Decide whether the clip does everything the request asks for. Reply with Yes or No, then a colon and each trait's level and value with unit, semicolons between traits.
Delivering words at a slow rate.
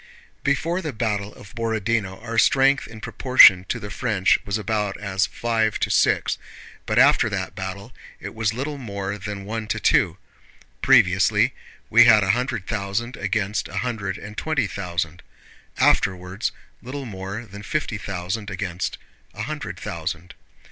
No: average, 150 wpm